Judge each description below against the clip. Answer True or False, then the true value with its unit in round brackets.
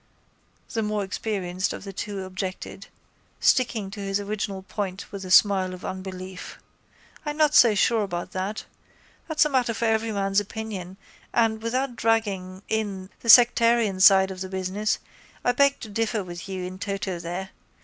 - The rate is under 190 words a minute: True (160 wpm)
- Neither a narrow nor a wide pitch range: True (3.0 semitones)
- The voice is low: False (200 Hz)